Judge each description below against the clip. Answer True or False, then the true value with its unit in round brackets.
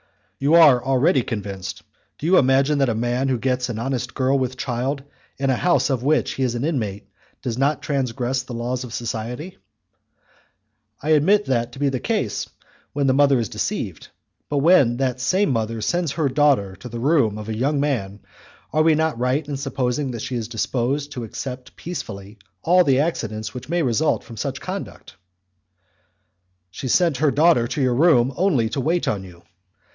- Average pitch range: True (3.7 semitones)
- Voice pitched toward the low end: True (130 Hz)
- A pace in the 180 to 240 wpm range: True (190 wpm)